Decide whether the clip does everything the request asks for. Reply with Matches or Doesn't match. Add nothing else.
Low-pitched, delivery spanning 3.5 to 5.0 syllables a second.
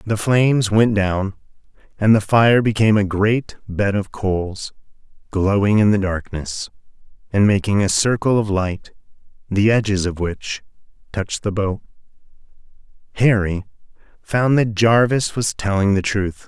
Matches